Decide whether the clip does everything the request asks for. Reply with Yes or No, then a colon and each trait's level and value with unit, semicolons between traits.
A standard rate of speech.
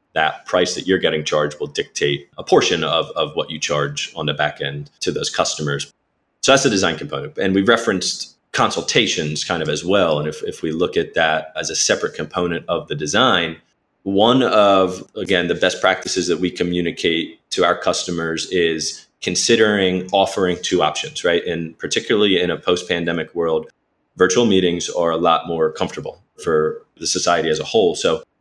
Yes: average, 185 wpm